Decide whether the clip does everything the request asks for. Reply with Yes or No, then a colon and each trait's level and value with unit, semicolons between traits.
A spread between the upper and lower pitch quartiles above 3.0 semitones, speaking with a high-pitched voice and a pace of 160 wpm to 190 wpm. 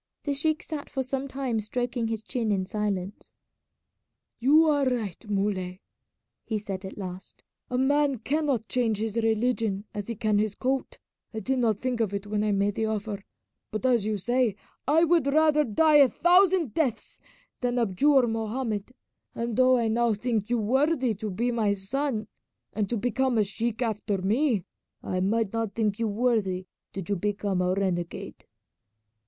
Yes: average, 3.9 semitones; high, 225 Hz; average, 170 wpm